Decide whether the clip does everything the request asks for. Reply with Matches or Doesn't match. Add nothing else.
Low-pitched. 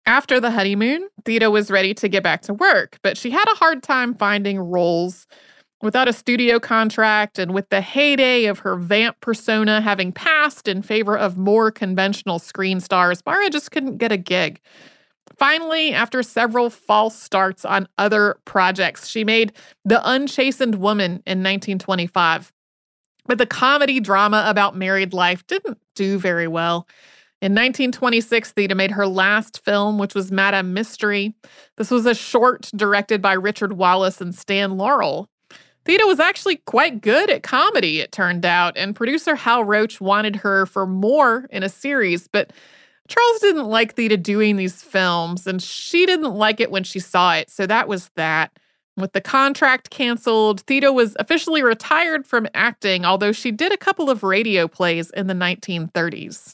Doesn't match